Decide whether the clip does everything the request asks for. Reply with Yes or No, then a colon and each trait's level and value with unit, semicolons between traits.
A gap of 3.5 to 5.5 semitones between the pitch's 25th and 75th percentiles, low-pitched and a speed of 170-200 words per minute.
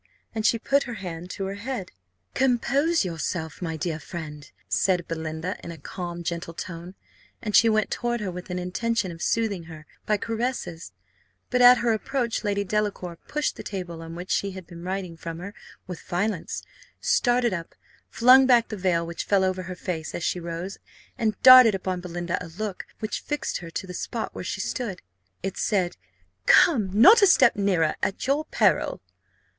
No: average, 4.9 semitones; high, 190 Hz; average, 185 wpm